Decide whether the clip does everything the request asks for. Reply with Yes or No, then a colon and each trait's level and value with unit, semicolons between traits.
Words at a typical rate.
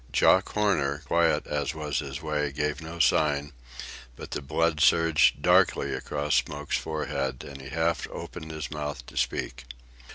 Yes: average, 155 wpm